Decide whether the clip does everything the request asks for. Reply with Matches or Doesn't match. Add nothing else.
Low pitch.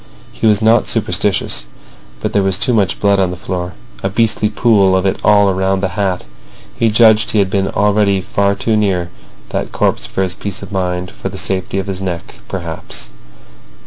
Matches